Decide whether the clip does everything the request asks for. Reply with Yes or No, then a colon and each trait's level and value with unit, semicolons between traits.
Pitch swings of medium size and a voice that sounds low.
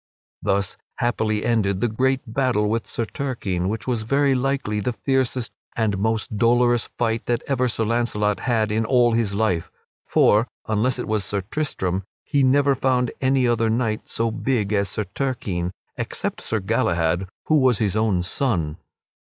Yes: average, 3.4 semitones; low, 115 Hz